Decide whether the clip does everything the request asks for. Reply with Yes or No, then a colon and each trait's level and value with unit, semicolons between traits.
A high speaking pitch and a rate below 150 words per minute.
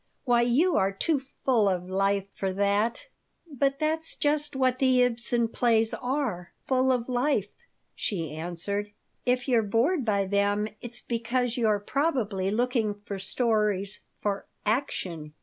Yes: high, 225 Hz; average, 140 wpm